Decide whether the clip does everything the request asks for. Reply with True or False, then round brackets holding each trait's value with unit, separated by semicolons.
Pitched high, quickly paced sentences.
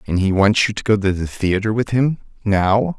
False (105 Hz; 220 wpm)